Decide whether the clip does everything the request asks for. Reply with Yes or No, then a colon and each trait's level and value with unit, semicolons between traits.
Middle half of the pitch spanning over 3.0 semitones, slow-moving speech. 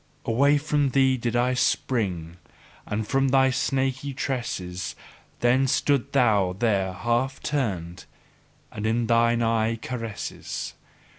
Yes: average, 3.7 semitones; slow, 120 wpm